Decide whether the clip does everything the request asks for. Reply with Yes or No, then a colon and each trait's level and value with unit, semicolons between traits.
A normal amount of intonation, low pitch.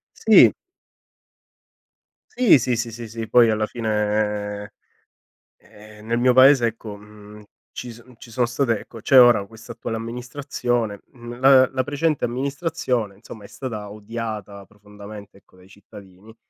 Yes: average, 3.0 semitones; low, 115 Hz